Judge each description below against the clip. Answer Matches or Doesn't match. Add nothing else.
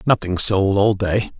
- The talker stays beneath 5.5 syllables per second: Matches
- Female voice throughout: Doesn't match